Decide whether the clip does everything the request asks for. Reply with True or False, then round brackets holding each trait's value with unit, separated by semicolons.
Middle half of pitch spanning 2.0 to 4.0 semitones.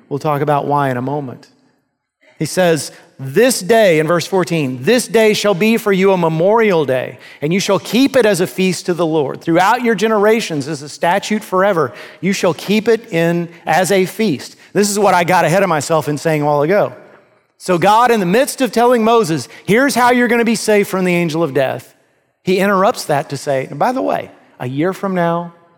False (4.8 semitones)